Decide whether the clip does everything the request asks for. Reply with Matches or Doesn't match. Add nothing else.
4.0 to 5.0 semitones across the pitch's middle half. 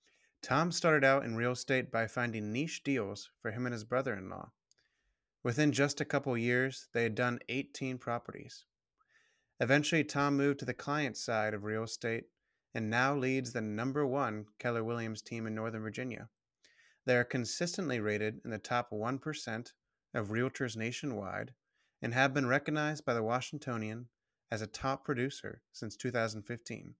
Doesn't match